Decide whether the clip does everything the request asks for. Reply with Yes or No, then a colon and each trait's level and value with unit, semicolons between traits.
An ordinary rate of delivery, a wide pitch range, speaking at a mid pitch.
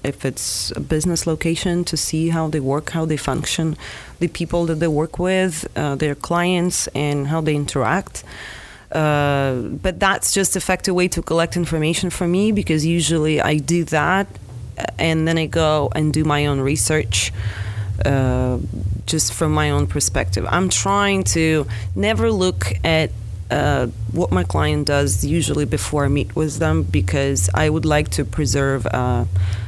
Yes: average, 165 wpm; wide, 7.0 semitones; medium, 150 Hz